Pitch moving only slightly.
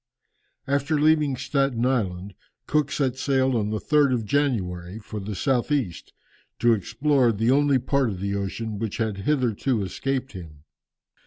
No: average, 5.3 semitones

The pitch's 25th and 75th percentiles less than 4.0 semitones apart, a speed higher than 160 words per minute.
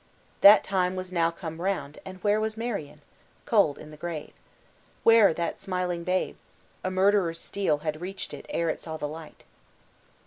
Yes: average, 3.5 semitones; average, 170 wpm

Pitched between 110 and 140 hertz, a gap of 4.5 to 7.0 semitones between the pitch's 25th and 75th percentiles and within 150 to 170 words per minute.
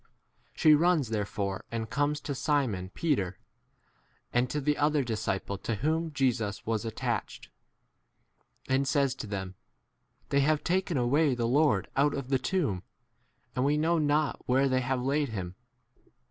Yes: low, 135 Hz; average, 4.8 semitones; average, 155 wpm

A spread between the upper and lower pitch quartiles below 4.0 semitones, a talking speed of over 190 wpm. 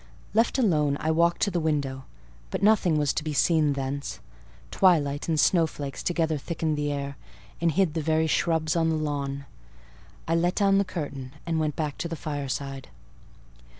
No: average, 2.9 semitones; average, 175 wpm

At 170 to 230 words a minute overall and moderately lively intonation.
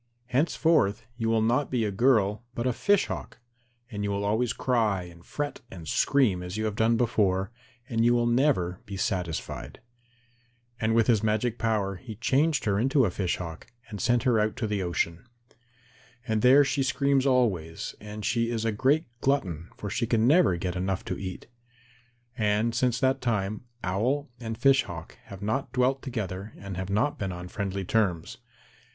Yes: average, 180 wpm; average, 4.3 semitones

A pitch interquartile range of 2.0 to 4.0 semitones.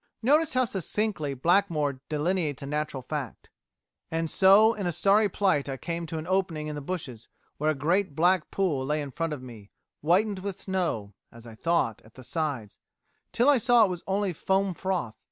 No: average, 5.2 semitones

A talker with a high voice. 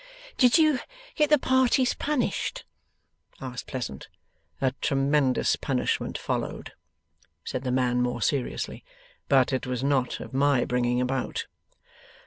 No: low, 135 Hz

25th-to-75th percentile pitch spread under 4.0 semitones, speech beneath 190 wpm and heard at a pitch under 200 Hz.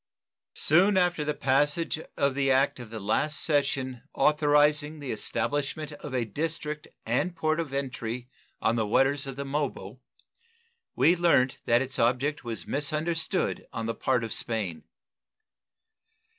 Yes: average, 3.5 semitones; average, 145 wpm; medium, 140 Hz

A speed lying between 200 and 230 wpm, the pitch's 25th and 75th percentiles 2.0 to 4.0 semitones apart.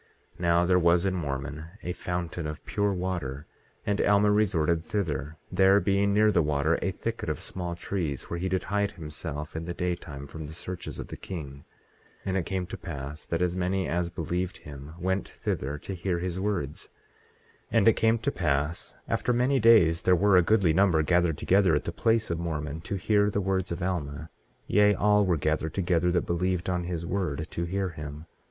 Yes: fast, 205 wpm; average, 3.5 semitones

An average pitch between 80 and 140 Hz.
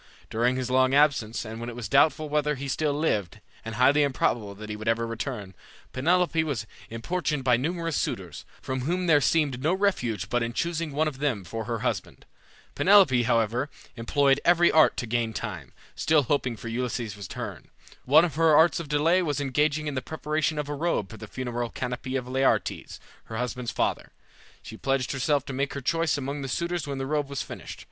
Yes: low, 135 Hz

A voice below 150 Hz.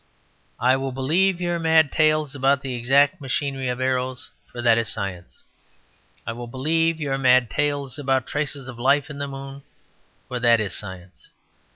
Yes: low, 135 Hz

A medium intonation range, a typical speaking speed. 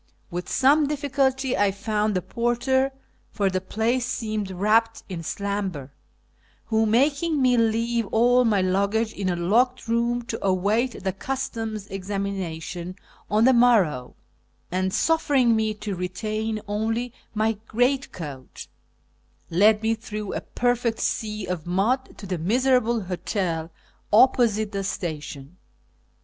No: average, 4.1 semitones; slow, 130 wpm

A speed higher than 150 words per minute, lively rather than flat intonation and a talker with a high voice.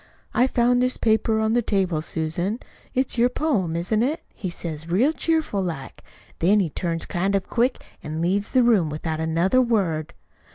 Yes: average, 175 wpm; wide, 6.3 semitones; high, 195 Hz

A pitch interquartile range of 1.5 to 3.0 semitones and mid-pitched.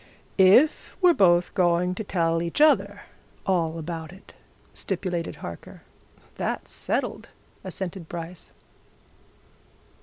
Yes: narrow, 2.4 semitones; medium, 175 Hz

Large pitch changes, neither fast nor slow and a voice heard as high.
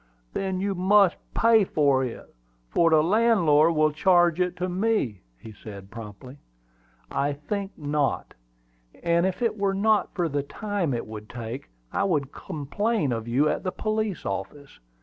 No: wide, 6.0 semitones; average, 160 wpm; medium, 165 Hz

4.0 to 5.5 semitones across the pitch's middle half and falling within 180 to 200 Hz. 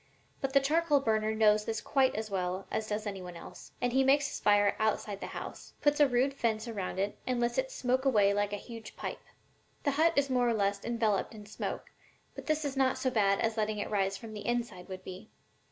No: average, 4.4 semitones; high, 220 Hz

